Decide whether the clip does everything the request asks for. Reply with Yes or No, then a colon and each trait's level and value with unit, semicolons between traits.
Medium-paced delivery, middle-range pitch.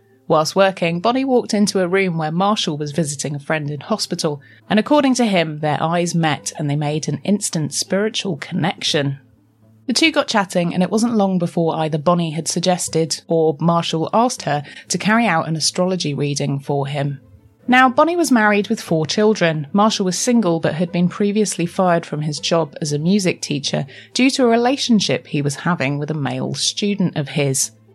Yes: average, 190 wpm; medium, 170 Hz